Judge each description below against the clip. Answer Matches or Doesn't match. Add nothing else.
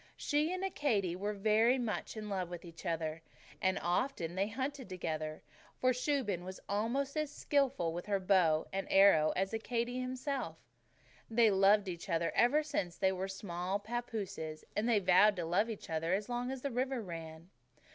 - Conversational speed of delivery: Matches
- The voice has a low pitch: Doesn't match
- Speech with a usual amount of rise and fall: Doesn't match